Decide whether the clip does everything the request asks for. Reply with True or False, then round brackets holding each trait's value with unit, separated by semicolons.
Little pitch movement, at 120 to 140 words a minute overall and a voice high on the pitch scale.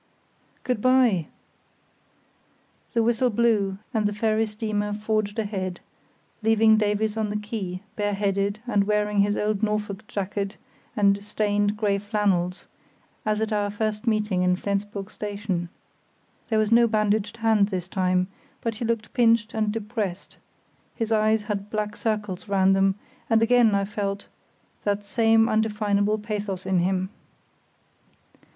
True (1.6 semitones; 135 wpm; 210 Hz)